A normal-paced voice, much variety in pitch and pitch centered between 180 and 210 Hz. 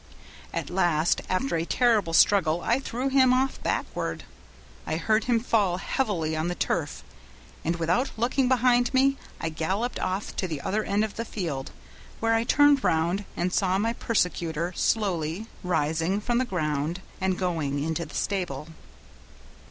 Yes: average, 160 wpm; wide, 5.9 semitones; high, 190 Hz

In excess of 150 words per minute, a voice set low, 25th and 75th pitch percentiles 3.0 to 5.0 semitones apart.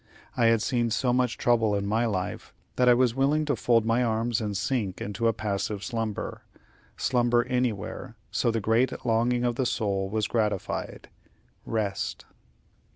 No: average, 160 wpm; low, 115 Hz; narrow, 2.4 semitones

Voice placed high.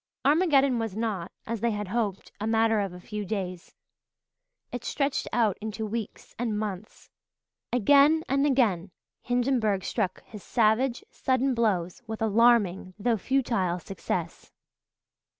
Yes: high, 220 Hz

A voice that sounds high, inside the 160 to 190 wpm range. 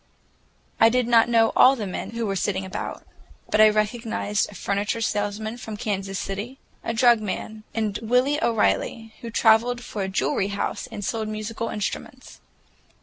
Yes: high, 220 Hz; average, 165 wpm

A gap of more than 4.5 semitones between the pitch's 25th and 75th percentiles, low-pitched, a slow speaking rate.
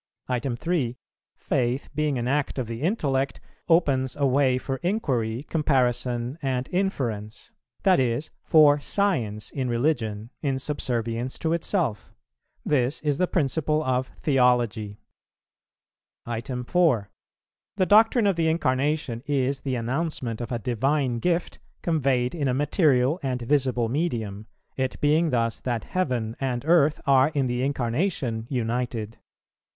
No: average, 4.0 semitones; low, 130 Hz; slow, 130 wpm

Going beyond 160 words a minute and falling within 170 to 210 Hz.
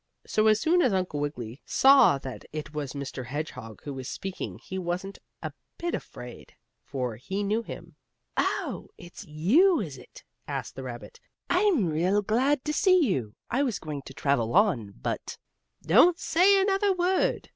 Yes: average, 170 wpm; medium, 185 Hz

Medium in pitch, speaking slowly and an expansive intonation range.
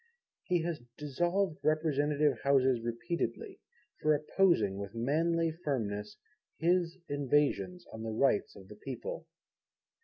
Yes: medium, 145 Hz; slow, 115 wpm; wide, 6.1 semitones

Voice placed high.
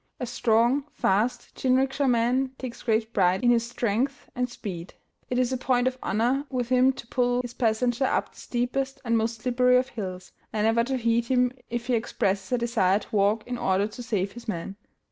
Yes: high, 240 Hz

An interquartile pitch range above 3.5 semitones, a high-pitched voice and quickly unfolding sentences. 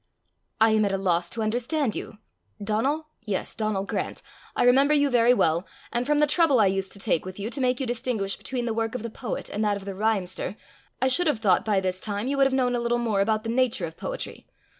Yes: average, 4.1 semitones; high, 225 Hz; fast, 245 wpm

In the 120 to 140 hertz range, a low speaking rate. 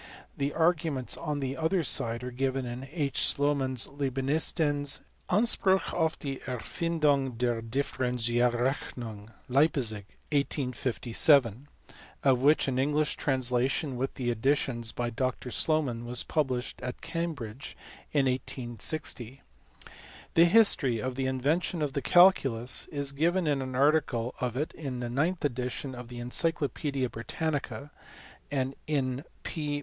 Yes: low, 135 Hz; slow, 130 wpm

